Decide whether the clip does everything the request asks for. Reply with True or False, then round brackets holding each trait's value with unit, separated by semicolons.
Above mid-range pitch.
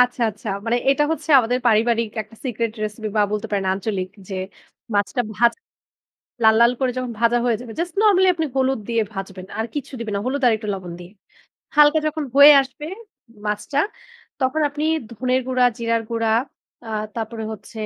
True (235 Hz)